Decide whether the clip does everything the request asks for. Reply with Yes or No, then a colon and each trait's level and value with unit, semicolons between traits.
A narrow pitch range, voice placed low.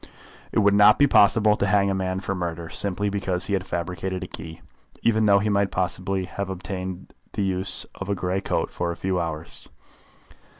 Yes: narrow, 1.9 semitones; very low, 95 Hz